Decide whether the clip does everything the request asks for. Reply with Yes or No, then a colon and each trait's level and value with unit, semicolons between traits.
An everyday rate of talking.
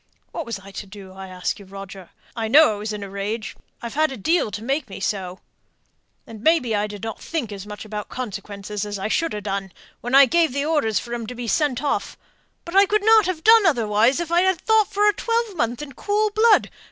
No: fast, 225 wpm